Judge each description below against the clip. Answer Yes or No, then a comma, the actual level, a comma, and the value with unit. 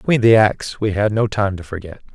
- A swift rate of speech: Yes, fast, 250 wpm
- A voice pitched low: Yes, low, 105 Hz